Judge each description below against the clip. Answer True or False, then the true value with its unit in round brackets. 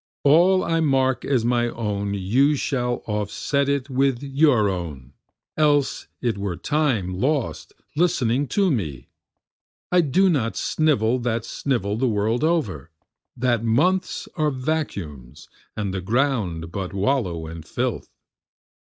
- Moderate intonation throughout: False (6.1 semitones)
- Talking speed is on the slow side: True (130 wpm)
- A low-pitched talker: True (120 Hz)